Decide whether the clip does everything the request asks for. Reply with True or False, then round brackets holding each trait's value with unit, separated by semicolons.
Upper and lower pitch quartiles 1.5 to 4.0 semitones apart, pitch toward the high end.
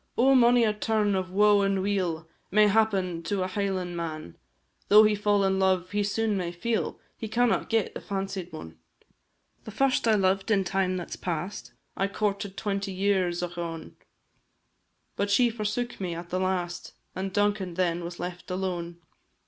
True (2.7 semitones; 195 Hz)